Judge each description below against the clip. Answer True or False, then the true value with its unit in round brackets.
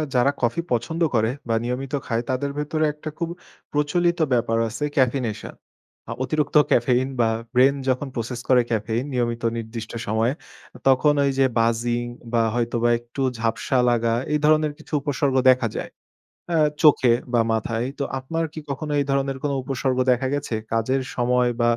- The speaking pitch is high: False (125 Hz)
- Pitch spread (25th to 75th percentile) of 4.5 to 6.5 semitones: False (3.3 semitones)